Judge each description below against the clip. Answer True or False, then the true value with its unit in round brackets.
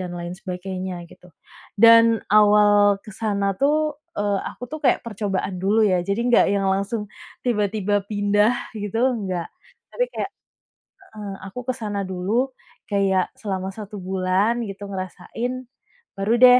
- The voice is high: True (205 Hz)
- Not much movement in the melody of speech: False (3.0 semitones)